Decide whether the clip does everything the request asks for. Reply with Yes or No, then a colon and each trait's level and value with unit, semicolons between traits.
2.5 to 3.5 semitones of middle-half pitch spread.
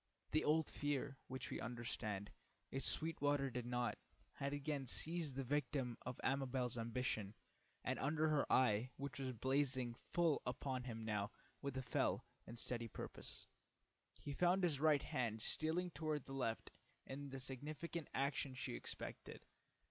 Yes: average, 3.0 semitones